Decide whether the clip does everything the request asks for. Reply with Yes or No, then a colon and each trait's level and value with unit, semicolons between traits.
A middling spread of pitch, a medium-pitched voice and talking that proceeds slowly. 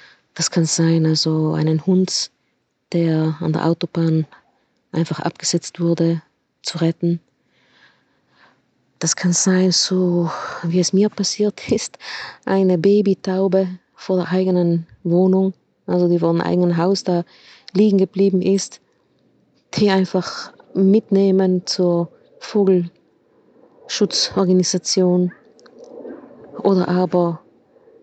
No: narrow, 2.2 semitones; medium, 180 Hz; slow, 100 wpm